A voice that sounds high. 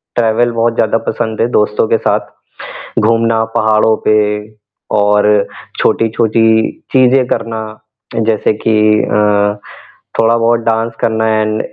No: low, 110 Hz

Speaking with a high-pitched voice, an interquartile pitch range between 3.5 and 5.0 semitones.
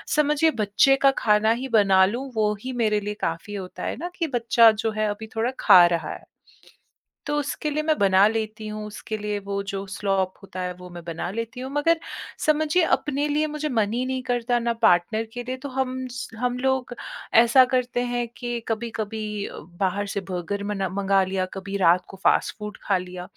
Yes: high, 220 Hz; average, 4.5 semitones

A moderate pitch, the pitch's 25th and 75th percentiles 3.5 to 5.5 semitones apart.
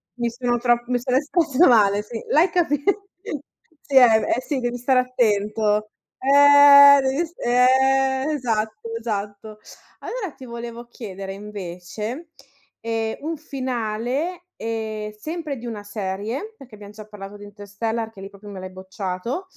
No: high, 235 Hz; average, 4.2 semitones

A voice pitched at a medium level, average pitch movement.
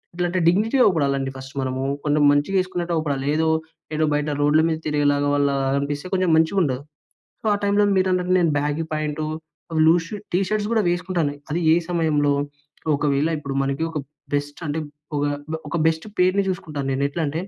Yes: medium, 155 Hz; average, 3.7 semitones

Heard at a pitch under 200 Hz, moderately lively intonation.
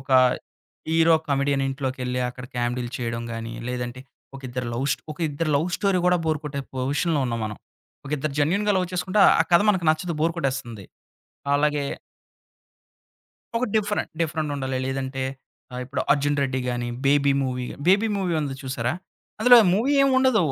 Yes: medium, 140 Hz; average, 4.7 semitones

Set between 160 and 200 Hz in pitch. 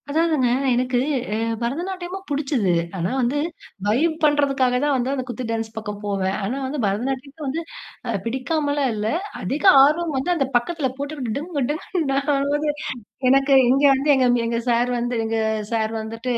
No: very high, 270 Hz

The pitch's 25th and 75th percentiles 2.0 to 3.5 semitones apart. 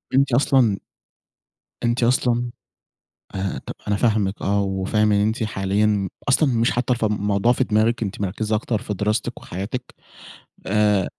Yes: average, 2.8 semitones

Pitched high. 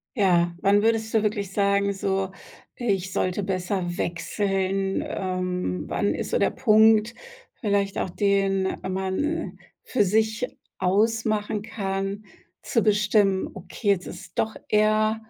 Yes: high, 200 Hz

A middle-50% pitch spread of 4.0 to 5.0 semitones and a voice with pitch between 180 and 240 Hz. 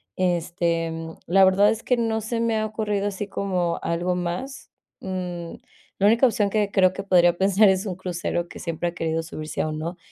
No: average, 3.2 semitones; medium, 185 Hz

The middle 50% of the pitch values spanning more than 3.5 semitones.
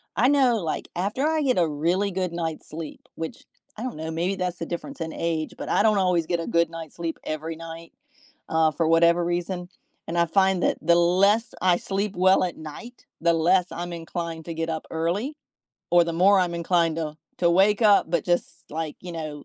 No: average, 2.7 semitones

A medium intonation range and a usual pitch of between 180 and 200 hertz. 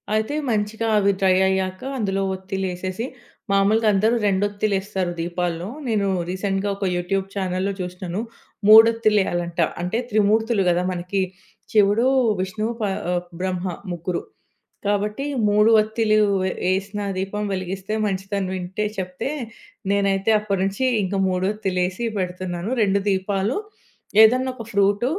No: narrow, 2.2 semitones; high, 195 Hz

